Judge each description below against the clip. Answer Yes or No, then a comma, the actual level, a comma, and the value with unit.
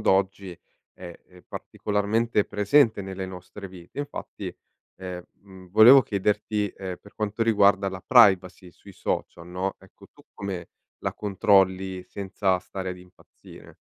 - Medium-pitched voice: No, very low, 95 Hz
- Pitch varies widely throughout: No, narrow, 1.9 semitones